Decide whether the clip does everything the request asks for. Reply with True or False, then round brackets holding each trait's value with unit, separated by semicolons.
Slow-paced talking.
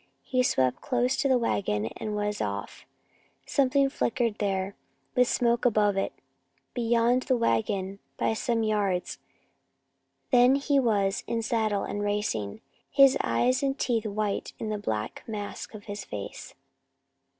False (145 wpm)